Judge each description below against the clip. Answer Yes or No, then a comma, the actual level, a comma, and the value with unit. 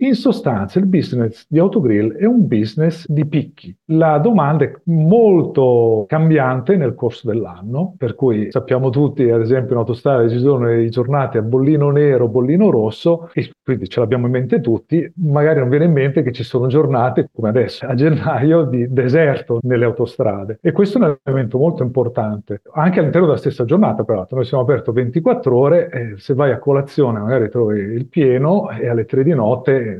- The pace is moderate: No, fast, 180 wpm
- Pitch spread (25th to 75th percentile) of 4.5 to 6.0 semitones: Yes, average, 5.1 semitones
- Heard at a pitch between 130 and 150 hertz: Yes, low, 135 Hz